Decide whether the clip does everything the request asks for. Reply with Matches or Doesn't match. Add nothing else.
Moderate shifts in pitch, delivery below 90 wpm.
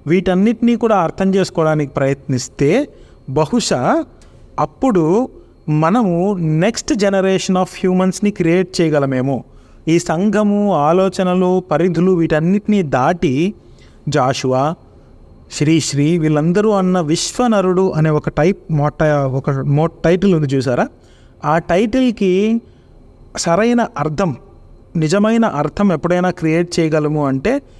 Doesn't match